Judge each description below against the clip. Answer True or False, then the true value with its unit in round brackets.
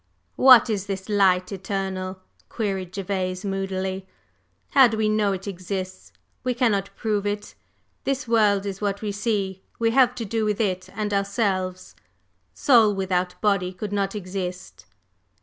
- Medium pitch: False (200 Hz)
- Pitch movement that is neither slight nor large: False (2.2 semitones)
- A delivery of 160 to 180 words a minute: False (150 wpm)